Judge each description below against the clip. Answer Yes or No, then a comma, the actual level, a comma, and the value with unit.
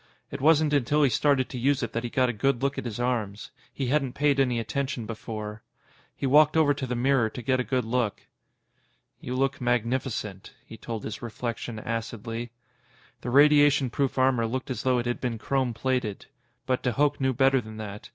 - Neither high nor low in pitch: No, low, 125 Hz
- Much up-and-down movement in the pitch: No, average, 3.0 semitones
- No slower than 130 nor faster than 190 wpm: No, average, 200 wpm